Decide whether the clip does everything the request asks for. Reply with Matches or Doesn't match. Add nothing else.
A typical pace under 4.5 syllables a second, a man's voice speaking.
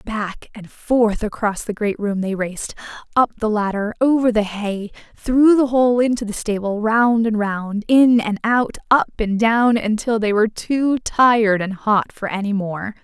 Doesn't match